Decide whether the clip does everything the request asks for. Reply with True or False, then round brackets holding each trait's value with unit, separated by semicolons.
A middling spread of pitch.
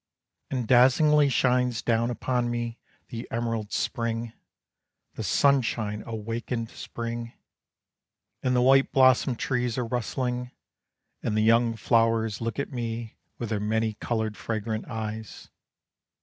False (1.8 semitones)